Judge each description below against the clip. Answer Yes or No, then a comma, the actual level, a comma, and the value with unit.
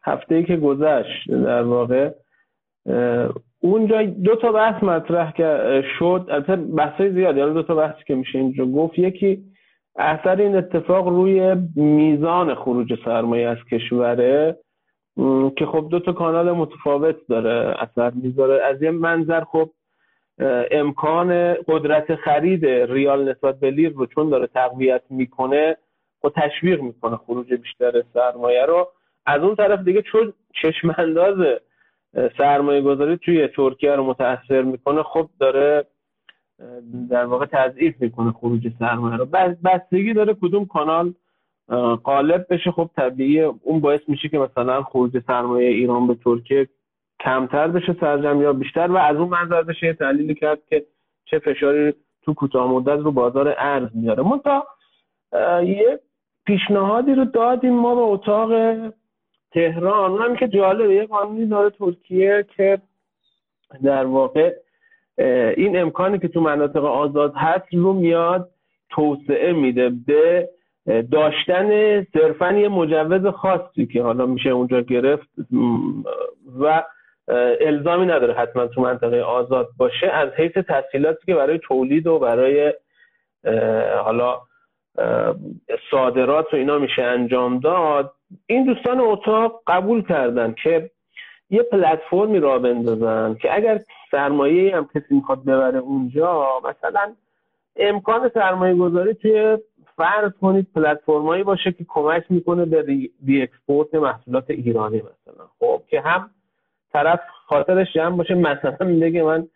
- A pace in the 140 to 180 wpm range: No, average, 130 wpm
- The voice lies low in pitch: No, medium, 160 Hz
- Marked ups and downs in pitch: Yes, wide, 5.8 semitones